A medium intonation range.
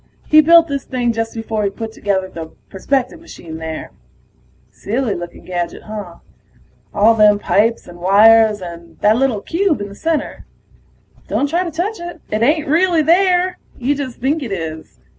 No: wide, 7.6 semitones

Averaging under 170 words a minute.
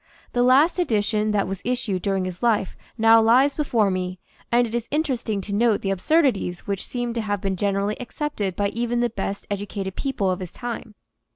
No: average, 195 wpm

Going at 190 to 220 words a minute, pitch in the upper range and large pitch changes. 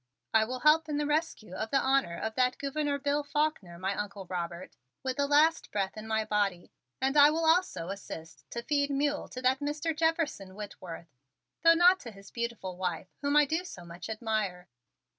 Yes: average, 195 wpm; very high, 255 Hz; wide, 7.0 semitones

